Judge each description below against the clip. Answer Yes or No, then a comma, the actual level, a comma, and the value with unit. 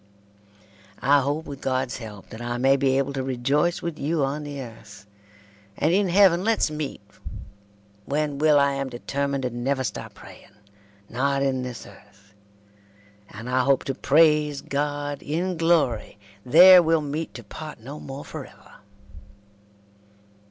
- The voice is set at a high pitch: No, medium, 140 Hz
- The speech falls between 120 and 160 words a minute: Yes, average, 150 wpm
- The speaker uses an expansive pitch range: No, average, 3.0 semitones